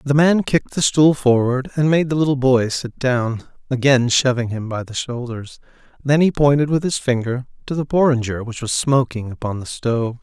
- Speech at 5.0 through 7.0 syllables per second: Yes, 5.1 syllables/s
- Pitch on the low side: Yes, low, 130 Hz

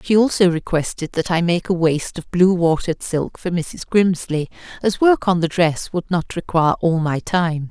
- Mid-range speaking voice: Yes, medium, 175 Hz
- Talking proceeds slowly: No, average, 200 wpm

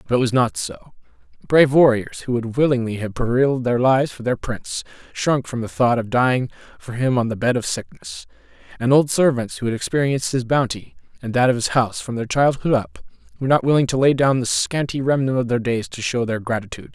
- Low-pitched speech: Yes, low, 125 Hz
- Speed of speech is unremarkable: No, fast, 225 wpm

